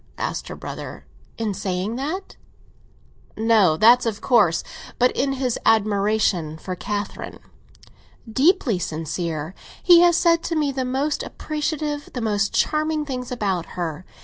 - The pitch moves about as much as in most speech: No, wide, 7.4 semitones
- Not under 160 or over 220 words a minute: No, slow, 135 wpm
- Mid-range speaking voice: No, high, 225 Hz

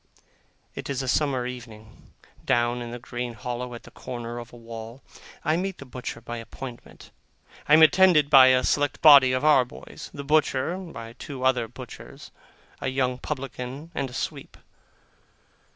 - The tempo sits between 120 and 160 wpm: No, average, 170 wpm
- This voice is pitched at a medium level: No, low, 130 Hz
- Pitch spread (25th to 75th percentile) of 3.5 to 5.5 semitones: No, average, 2.9 semitones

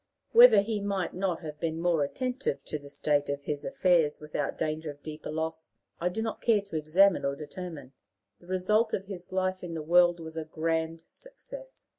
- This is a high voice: No, medium, 170 Hz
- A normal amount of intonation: Yes, average, 4.2 semitones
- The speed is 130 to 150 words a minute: No, average, 195 wpm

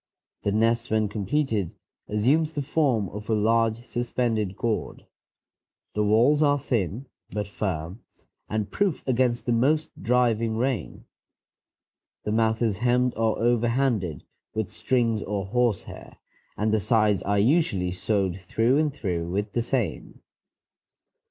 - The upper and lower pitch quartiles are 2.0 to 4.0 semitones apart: Yes, average, 3.2 semitones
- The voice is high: No, low, 115 Hz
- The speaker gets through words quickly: No, slow, 135 wpm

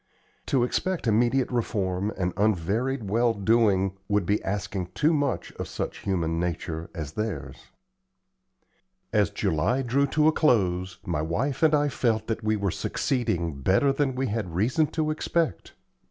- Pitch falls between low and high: No, low, 110 Hz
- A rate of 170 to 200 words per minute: No, average, 155 wpm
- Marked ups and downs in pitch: Yes, wide, 6.3 semitones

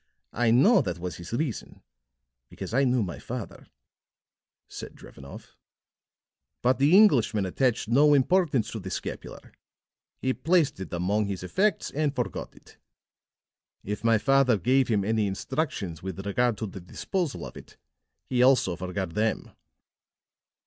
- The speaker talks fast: No, average, 140 wpm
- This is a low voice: Yes, low, 115 Hz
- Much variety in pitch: Yes, wide, 6.0 semitones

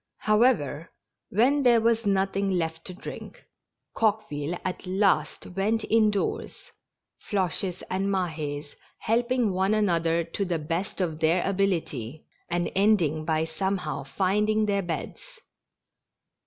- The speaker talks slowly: Yes, slow, 125 wpm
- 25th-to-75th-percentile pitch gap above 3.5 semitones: Yes, average, 4.3 semitones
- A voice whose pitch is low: No, high, 190 Hz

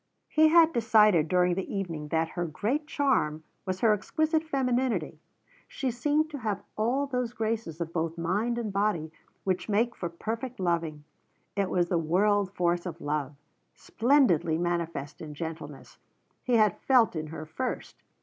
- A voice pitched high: Yes, high, 195 Hz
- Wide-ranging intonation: Yes, wide, 6.3 semitones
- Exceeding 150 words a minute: Yes, average, 160 wpm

